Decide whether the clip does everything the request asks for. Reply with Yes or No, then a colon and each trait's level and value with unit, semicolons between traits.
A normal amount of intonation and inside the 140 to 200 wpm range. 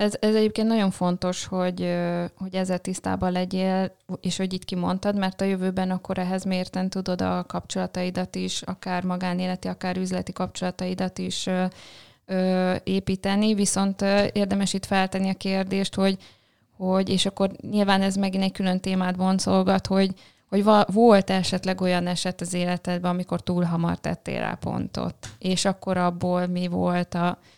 No: narrow, 1.1 semitones; average, 150 wpm